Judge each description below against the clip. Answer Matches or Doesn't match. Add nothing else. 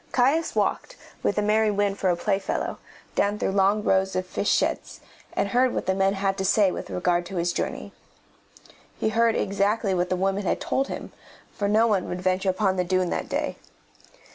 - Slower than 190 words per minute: Doesn't match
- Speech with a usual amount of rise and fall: Doesn't match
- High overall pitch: Matches